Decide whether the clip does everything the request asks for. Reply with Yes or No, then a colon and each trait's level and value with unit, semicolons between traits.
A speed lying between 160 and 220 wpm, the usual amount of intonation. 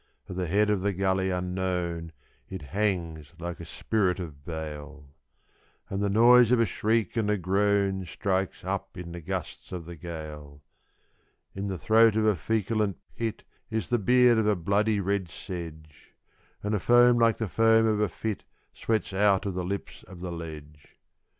Yes: average, 175 wpm; average, 3.9 semitones